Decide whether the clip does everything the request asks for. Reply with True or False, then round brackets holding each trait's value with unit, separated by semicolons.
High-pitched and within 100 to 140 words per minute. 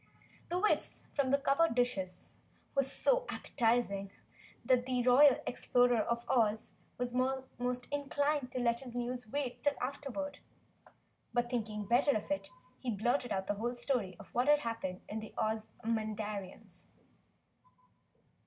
True (245 Hz; 135 wpm)